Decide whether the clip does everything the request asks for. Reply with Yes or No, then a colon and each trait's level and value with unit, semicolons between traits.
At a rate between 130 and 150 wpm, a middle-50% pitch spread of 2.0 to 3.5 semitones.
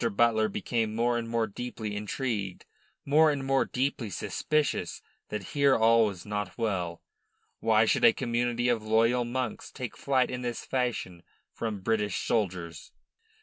Yes: average, 145 wpm; average, 2.9 semitones